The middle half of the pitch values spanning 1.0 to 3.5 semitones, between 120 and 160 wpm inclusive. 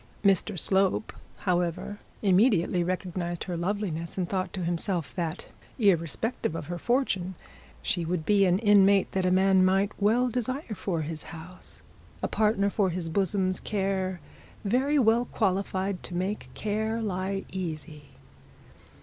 Yes: average, 2.7 semitones; average, 140 wpm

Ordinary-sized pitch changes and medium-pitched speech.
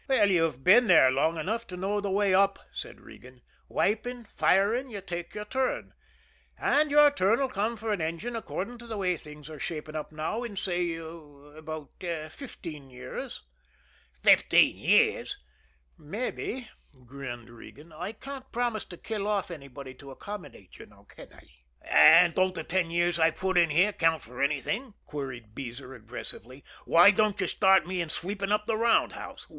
No: wide, 5.8 semitones; medium, 180 Hz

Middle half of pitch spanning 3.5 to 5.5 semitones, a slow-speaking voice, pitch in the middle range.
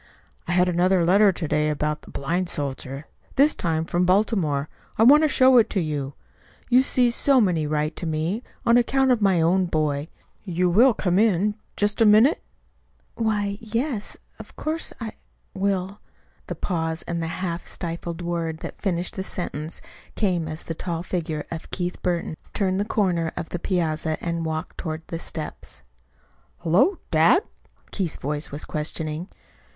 No: average, 4.5 semitones; average, 165 wpm; medium, 175 Hz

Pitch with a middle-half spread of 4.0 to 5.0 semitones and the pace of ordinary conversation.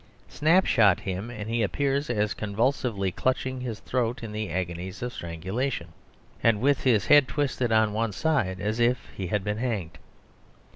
Yes: average, 4.5 semitones; average, 160 wpm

